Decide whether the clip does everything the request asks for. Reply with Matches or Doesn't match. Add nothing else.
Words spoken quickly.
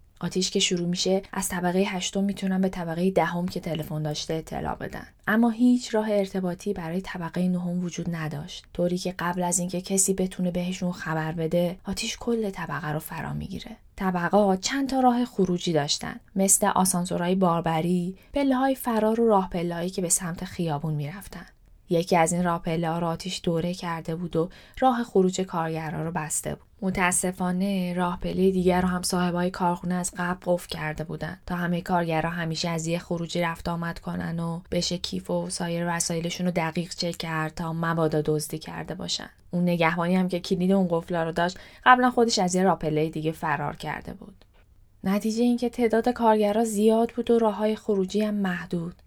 Matches